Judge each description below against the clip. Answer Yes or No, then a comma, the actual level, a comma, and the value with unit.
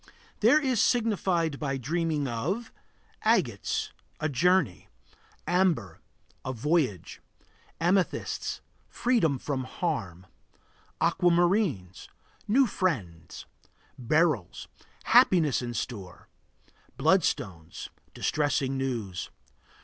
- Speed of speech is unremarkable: No, slow, 80 wpm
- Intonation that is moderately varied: No, wide, 7.2 semitones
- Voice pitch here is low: No, medium, 150 Hz